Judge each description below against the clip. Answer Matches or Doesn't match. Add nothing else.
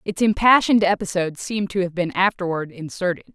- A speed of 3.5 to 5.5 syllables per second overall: Doesn't match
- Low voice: Doesn't match